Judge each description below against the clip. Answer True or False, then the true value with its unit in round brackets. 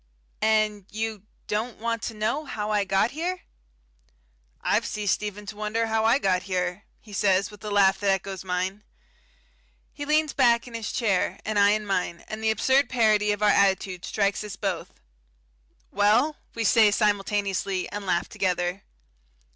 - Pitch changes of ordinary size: False (2.2 semitones)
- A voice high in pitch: True (210 Hz)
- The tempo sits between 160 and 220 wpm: True (165 wpm)